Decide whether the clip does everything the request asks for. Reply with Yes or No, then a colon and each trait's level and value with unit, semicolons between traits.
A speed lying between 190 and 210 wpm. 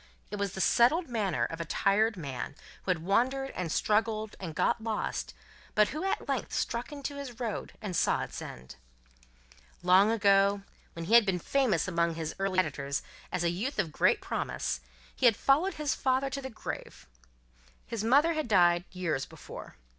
No: average, 180 wpm